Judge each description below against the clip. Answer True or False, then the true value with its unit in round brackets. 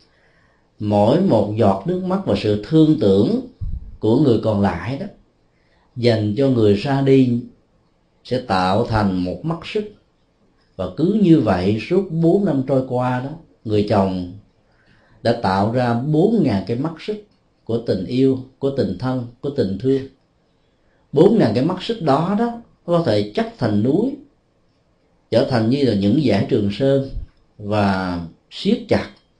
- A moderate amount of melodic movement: False (6.6 semitones)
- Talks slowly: True (155 wpm)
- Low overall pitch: True (120 Hz)